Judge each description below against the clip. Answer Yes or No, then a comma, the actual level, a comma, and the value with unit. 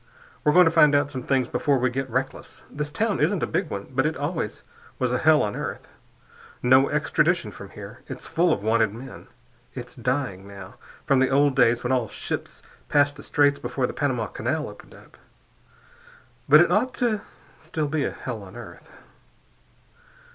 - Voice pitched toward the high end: No, low, 135 Hz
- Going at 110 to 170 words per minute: No, average, 185 wpm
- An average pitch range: Yes, average, 3.5 semitones